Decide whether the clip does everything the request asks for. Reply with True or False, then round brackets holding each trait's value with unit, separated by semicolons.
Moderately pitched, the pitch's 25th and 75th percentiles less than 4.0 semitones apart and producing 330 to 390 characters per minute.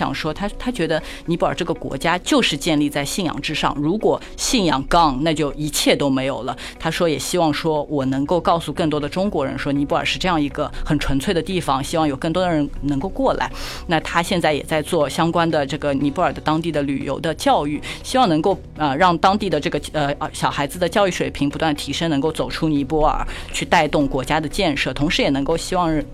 True (155 Hz; 2.9 semitones; 340 characters per minute)